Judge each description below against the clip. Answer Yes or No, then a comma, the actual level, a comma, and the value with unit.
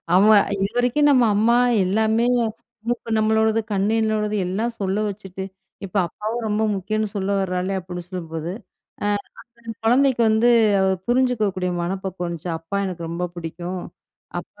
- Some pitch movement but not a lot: Yes, average, 3.3 semitones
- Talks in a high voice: Yes, high, 205 Hz